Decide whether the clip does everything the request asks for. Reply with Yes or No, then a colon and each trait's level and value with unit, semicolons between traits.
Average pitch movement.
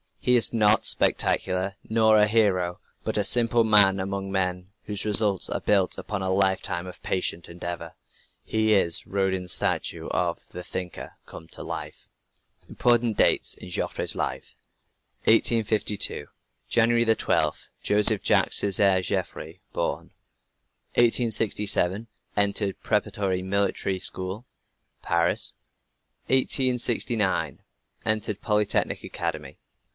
Yes: average, 3.0 semitones